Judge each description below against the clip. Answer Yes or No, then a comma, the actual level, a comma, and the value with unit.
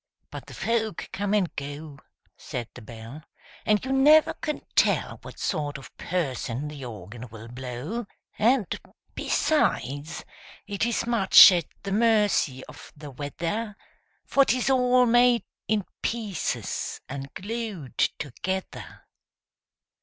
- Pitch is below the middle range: No, high, 190 Hz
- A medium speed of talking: No, slow, 125 wpm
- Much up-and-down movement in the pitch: Yes, wide, 8.8 semitones